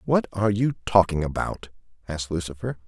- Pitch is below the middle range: Yes, very low, 95 Hz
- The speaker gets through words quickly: No, average, 145 wpm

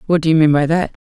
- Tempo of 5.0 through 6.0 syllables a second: No, 7.3 syllables/s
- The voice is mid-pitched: Yes, medium, 160 Hz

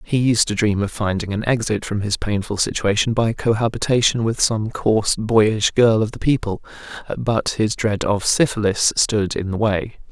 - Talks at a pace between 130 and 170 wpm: No, average, 185 wpm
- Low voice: Yes, low, 110 Hz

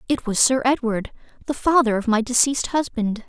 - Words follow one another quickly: No, average, 185 wpm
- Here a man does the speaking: No, female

